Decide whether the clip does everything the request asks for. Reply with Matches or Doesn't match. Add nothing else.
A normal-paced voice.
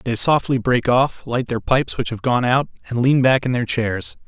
Doesn't match